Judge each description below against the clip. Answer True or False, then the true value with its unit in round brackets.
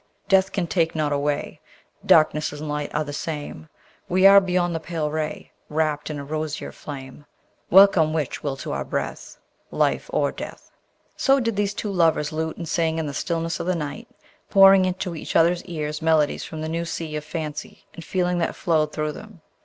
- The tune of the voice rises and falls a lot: False (2.8 semitones)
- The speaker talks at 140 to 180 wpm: False (190 wpm)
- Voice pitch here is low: False (160 Hz)